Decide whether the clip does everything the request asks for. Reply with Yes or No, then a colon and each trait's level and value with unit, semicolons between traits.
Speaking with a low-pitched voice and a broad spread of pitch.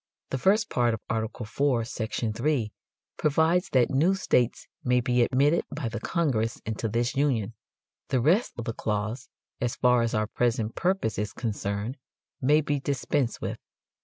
No: low, 125 Hz; average, 4.3 semitones